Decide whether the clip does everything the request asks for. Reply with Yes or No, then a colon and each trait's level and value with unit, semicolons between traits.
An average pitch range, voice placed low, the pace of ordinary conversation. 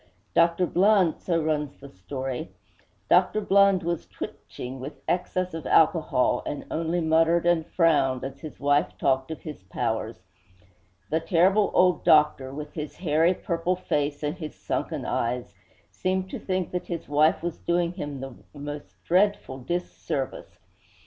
No: average, 3.6 semitones; medium, 160 Hz; average, 150 wpm